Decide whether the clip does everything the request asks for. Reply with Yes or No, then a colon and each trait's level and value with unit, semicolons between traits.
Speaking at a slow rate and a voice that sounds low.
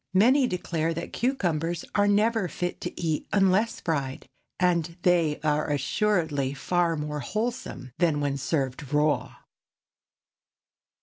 No: slow, 120 wpm; medium, 165 Hz